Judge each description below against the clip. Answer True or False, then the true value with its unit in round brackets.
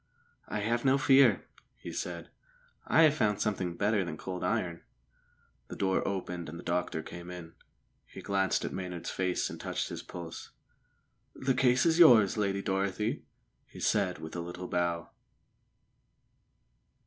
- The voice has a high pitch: False (95 Hz)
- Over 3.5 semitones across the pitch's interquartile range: True (3.9 semitones)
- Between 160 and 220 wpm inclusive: False (150 wpm)